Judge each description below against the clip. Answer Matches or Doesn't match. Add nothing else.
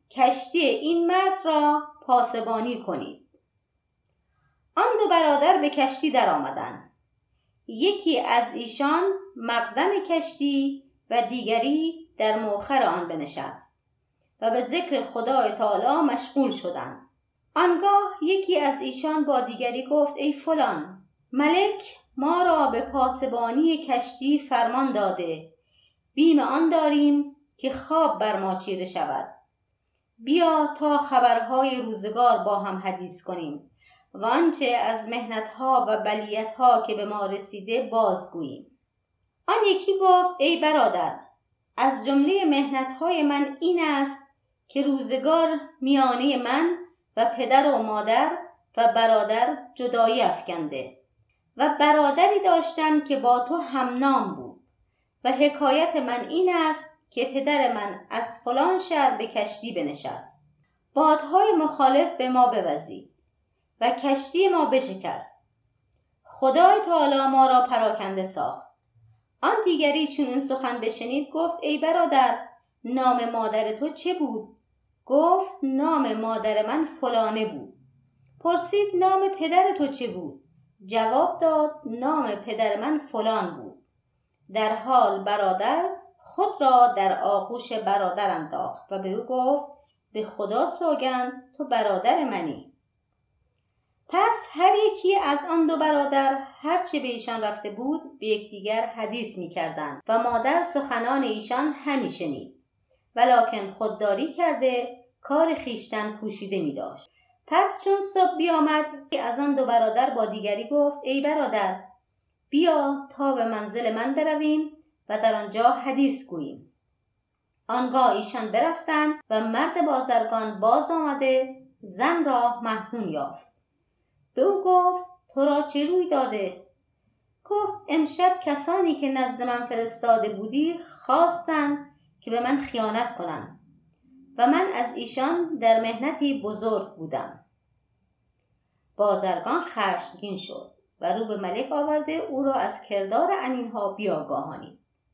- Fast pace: Doesn't match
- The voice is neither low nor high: Doesn't match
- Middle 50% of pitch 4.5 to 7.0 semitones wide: Matches